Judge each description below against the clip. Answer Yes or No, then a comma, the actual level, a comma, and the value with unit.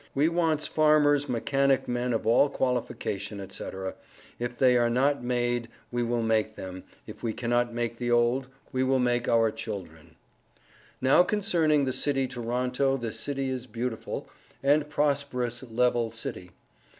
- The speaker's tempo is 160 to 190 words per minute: No, average, 150 wpm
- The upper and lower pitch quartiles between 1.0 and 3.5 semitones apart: Yes, average, 2.8 semitones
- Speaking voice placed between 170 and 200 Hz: No, low, 125 Hz